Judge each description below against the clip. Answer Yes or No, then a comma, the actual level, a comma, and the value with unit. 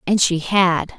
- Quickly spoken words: No, average, 185 wpm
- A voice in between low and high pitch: Yes, medium, 180 Hz